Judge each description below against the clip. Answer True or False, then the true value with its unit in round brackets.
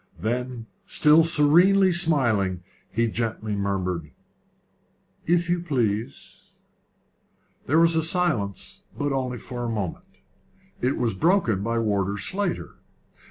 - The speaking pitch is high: False (125 Hz)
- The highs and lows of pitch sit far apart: True (8.0 semitones)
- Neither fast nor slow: False (115 wpm)